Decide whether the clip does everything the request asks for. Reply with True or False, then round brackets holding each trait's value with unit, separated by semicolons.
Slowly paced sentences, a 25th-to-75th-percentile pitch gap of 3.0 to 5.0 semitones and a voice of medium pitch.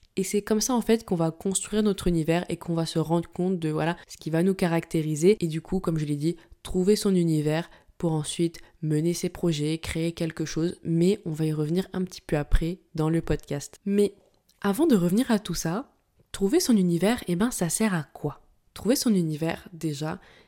False (220 wpm; 3.4 semitones; 170 Hz)